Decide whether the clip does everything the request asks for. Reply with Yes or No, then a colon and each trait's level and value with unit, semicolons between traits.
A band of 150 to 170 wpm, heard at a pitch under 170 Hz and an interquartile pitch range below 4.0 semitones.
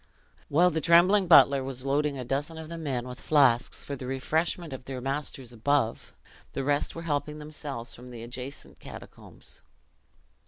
Yes: average, 165 wpm; medium, 140 Hz; average, 3.2 semitones